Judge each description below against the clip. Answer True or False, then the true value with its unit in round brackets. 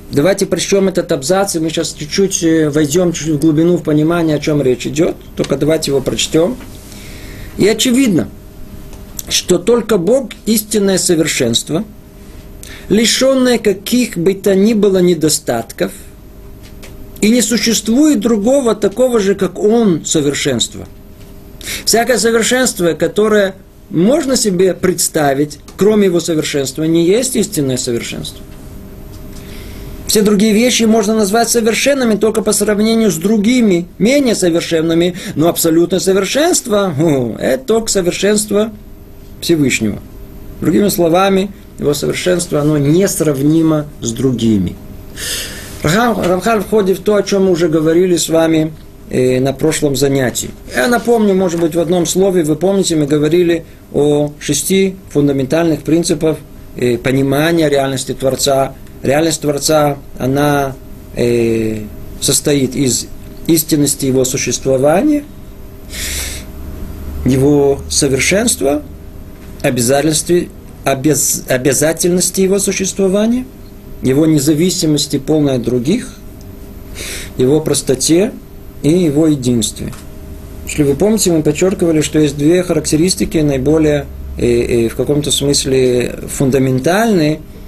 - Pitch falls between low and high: True (155 Hz)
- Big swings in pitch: True (6.6 semitones)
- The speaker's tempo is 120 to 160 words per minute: False (110 wpm)